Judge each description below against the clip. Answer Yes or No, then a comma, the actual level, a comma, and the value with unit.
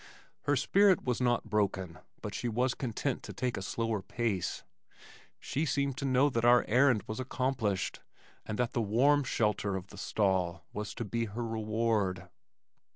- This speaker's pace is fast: No, average, 165 wpm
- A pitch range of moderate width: Yes, average, 3.7 semitones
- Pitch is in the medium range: No, low, 115 Hz